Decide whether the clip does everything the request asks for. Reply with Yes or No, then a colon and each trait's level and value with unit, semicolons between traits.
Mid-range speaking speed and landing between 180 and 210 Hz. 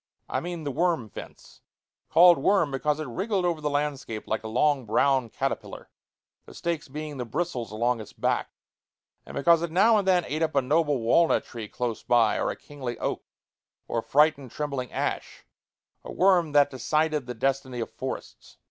No: average, 180 wpm; medium, 145 Hz